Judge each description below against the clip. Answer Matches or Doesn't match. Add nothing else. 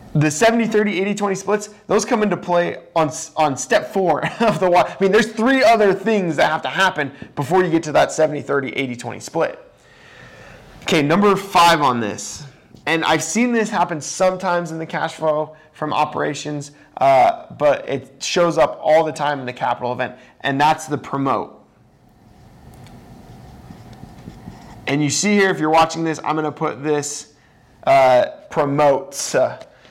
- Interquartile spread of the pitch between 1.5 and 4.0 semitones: Doesn't match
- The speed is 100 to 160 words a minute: Doesn't match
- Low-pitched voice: Doesn't match